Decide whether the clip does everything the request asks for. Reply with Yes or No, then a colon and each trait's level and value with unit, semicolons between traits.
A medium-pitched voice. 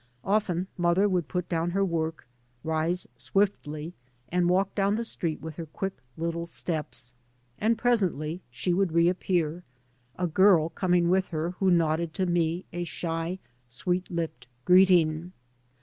Yes: medium, 175 Hz